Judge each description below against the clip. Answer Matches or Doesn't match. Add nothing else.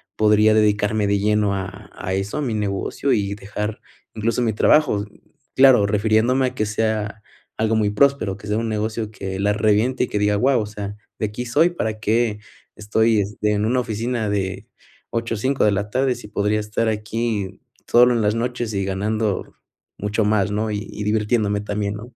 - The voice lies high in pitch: Doesn't match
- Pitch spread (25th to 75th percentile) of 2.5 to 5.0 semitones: Doesn't match